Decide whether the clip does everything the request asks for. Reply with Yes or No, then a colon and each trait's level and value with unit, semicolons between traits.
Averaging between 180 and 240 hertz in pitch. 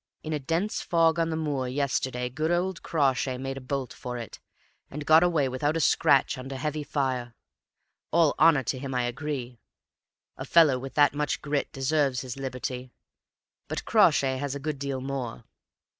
No: medium, 140 Hz